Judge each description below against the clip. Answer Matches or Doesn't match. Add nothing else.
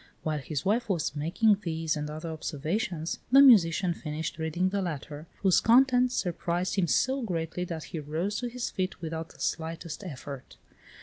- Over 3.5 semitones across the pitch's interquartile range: Matches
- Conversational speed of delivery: Matches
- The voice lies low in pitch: Doesn't match